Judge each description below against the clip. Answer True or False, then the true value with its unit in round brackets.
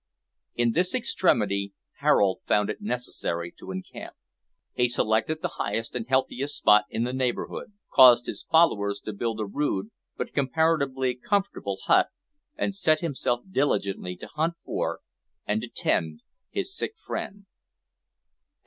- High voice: False (125 Hz)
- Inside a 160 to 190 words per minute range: False (140 wpm)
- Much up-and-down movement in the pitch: True (7.4 semitones)